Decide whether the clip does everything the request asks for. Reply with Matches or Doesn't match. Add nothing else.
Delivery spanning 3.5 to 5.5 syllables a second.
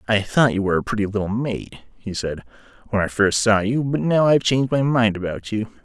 Doesn't match